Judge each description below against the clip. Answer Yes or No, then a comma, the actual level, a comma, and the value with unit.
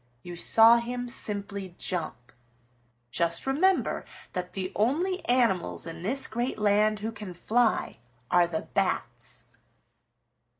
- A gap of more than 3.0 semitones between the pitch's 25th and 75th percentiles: Yes, average, 5.3 semitones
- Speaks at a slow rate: Yes, slow, 120 wpm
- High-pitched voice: Yes, high, 210 Hz